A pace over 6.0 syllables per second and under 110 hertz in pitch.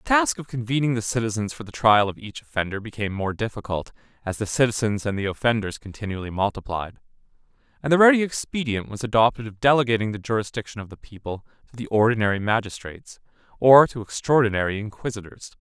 No: 6.4 syllables/s; low, 115 Hz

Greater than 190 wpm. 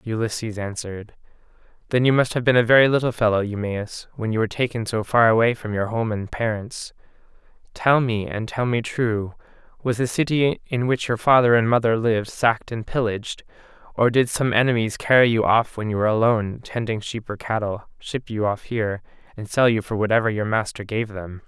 Yes: average, 200 wpm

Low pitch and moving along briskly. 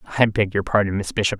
Yes: low, 100 Hz; fast, 255 wpm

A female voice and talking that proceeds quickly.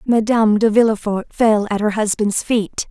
No: female; average, 165 wpm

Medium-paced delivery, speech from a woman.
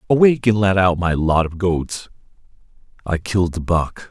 No: average, 175 wpm; male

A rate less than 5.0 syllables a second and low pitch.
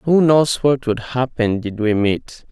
Yes: 3.7 syllables/s; low, 125 Hz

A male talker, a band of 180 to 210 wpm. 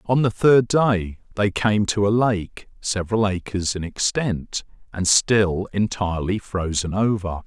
No: male; average, 145 wpm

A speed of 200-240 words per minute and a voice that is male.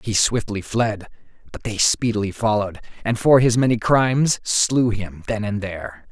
No: average, 165 wpm; male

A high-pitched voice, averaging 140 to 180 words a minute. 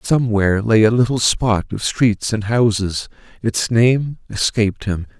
No: low, 110 Hz; average, 150 wpm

